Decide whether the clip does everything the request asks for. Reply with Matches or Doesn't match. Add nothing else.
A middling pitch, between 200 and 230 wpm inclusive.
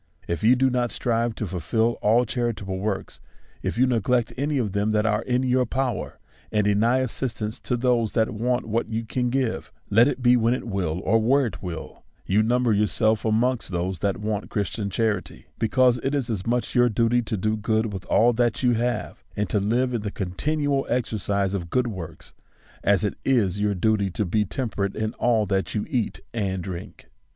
Doesn't match